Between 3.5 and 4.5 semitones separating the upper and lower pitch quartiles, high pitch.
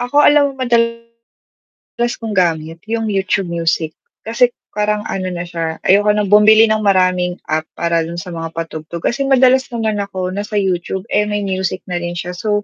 Yes: average, 4.2 semitones; high, 195 Hz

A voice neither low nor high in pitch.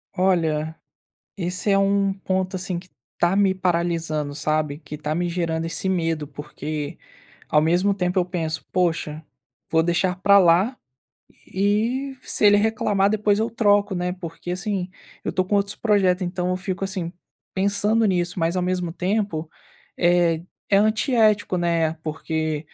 Yes: medium, 180 Hz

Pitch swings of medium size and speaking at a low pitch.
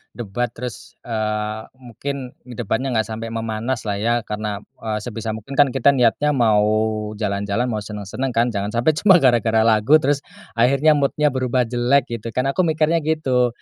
Yes: average, 3.5 semitones; low, 120 Hz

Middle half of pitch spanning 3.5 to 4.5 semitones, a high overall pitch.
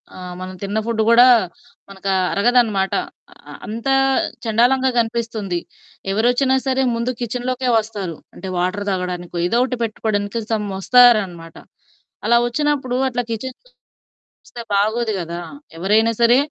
Yes: average, 3.8 semitones; high, 225 Hz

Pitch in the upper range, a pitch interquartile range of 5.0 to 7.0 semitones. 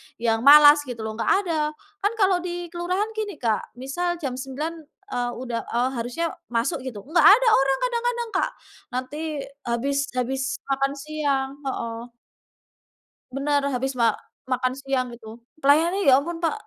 Yes: very high, 275 Hz; average, 5.3 semitones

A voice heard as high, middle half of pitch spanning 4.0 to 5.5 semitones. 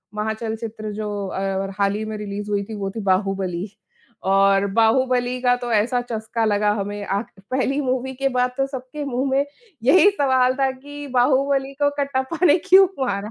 Yes: high, 235 Hz; average, 4.4 semitones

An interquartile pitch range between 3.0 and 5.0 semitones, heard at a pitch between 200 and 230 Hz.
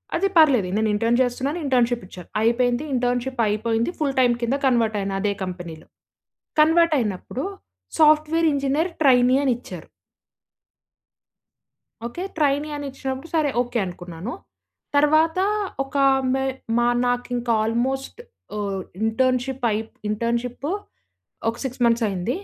No: average, 3.4 semitones; high, 245 Hz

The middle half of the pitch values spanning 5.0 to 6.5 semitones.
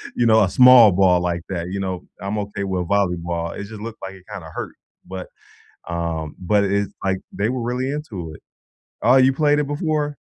Yes: average, 5.3 semitones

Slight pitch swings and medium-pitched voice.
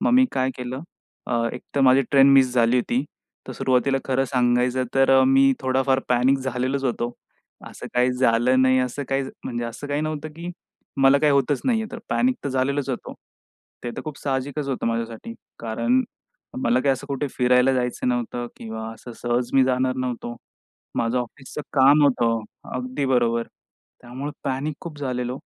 No: narrow, 2.0 semitones; low, 130 Hz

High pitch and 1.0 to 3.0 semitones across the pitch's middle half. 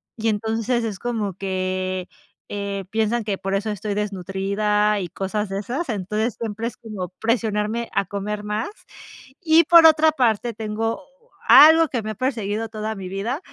Yes: high, 215 Hz; narrow, 2.6 semitones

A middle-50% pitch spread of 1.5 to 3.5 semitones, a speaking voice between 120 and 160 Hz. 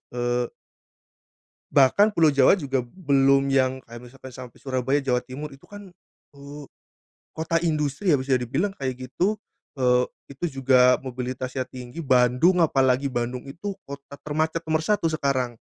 Yes: average, 3.1 semitones; low, 135 Hz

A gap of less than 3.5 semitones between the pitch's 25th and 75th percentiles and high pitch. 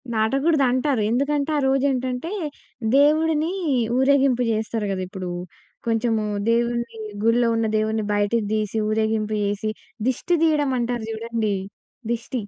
No: average, 3.8 semitones; high, 235 Hz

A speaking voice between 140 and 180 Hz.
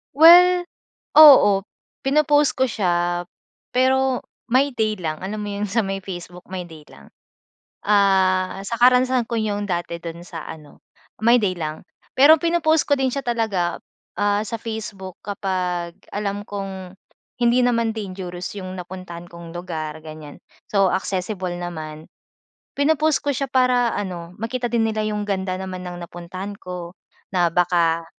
No: high, 195 Hz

